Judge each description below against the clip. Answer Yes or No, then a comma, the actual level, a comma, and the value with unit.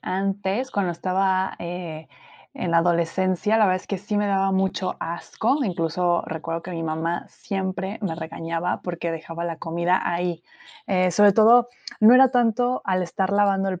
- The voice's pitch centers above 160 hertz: Yes, medium, 185 Hz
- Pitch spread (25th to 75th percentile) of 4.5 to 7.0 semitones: No, average, 2.8 semitones